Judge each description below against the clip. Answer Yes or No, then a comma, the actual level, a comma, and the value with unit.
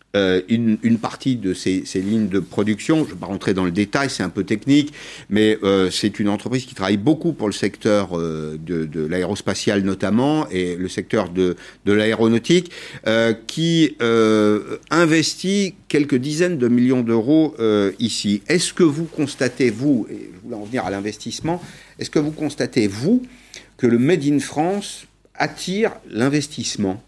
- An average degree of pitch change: No, wide, 6.6 semitones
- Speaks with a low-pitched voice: Yes, low, 115 Hz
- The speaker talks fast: No, average, 175 wpm